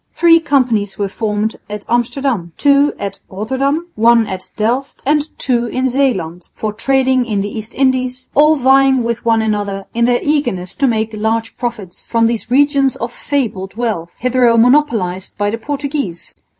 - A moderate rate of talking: Yes, average, 165 wpm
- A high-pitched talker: Yes, high, 235 Hz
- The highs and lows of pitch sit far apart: No, average, 4.3 semitones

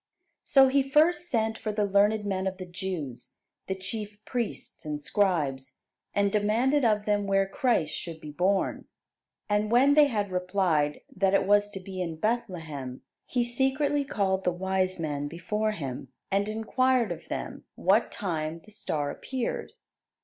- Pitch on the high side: Yes, high, 200 Hz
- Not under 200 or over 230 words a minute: No, average, 160 wpm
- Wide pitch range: No, average, 4.2 semitones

